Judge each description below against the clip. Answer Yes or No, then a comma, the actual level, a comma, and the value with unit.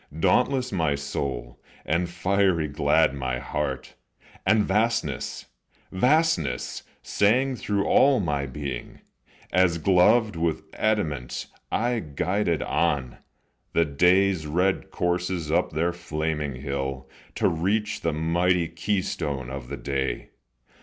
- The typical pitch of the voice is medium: No, very low, 85 Hz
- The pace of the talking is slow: Yes, slow, 110 wpm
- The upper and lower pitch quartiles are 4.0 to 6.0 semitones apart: Yes, wide, 5.4 semitones